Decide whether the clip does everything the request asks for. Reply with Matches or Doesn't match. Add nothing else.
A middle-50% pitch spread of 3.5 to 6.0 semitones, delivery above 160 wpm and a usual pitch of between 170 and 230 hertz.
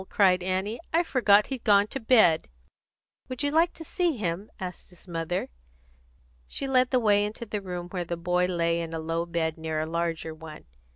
Matches